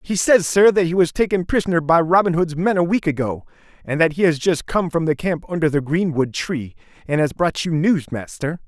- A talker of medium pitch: Yes, medium, 165 Hz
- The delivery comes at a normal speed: No, fast, 235 wpm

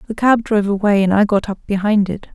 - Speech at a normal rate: No, fast, 255 wpm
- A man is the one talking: No, female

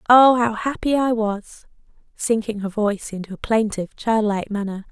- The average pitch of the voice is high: Yes, high, 220 Hz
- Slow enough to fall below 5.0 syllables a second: No, 5.1 syllables/s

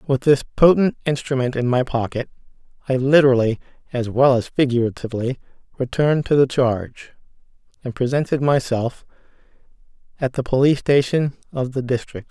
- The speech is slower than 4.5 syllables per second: No, 5.5 syllables/s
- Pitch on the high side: No, low, 130 Hz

